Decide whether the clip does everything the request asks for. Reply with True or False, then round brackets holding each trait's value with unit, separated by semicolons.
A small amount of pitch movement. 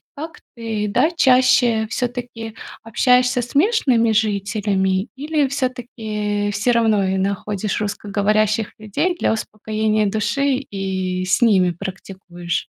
False (3.7 semitones)